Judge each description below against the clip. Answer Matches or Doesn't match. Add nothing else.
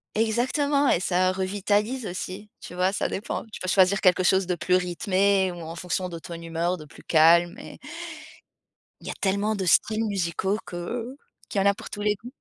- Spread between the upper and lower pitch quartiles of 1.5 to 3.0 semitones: Matches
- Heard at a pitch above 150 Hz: Matches